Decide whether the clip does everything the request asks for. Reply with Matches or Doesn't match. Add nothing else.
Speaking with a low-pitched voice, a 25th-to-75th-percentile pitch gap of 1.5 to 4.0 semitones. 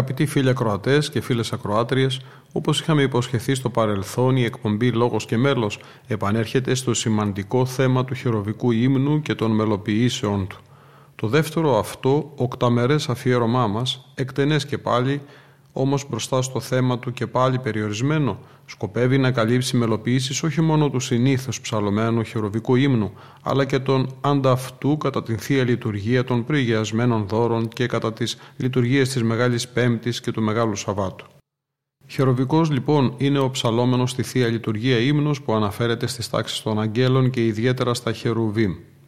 Matches